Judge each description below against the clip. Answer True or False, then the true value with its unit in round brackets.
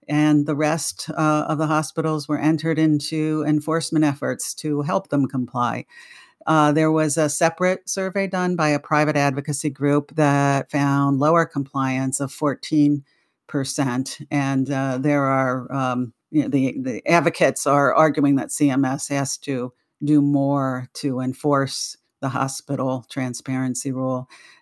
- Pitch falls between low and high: True (145 Hz)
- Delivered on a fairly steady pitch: True (2.3 semitones)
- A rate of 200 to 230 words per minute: False (135 wpm)